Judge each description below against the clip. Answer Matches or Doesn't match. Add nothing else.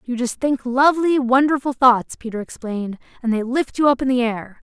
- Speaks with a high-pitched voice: Matches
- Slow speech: Doesn't match